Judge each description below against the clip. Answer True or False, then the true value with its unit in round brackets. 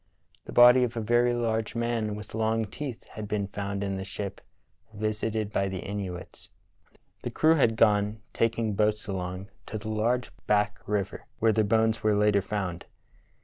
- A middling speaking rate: True (170 wpm)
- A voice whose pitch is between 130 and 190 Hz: False (105 Hz)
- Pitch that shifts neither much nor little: False (1.9 semitones)